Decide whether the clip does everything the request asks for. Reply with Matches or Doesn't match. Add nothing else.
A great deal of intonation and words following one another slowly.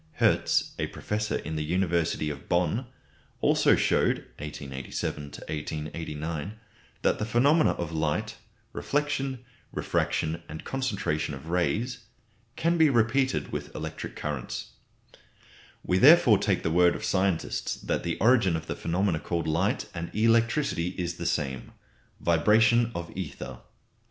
Matches